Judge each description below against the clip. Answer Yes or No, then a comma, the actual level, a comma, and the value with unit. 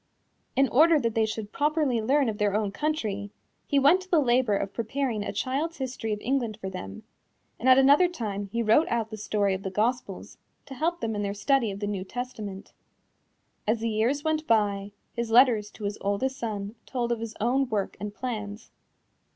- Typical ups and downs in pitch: Yes, average, 4.4 semitones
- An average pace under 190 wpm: No, average, 200 wpm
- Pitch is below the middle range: No, high, 230 Hz